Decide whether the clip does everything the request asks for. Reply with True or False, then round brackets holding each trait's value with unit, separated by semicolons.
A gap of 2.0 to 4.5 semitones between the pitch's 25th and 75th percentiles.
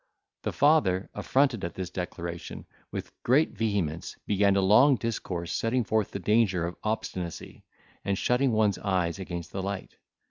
True (3.9 semitones)